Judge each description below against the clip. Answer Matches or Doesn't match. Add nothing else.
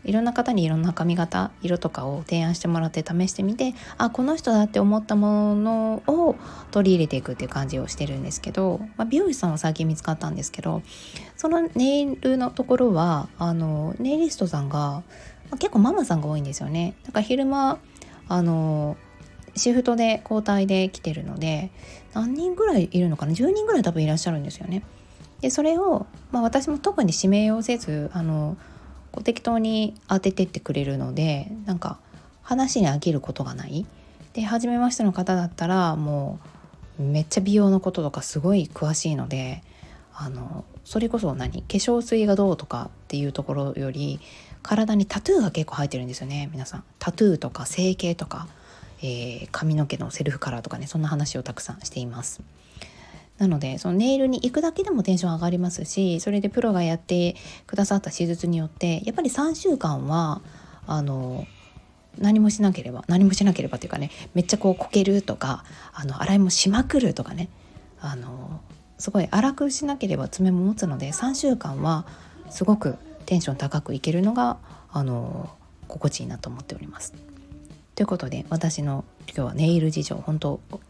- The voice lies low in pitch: Doesn't match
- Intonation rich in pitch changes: Matches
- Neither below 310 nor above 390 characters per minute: Matches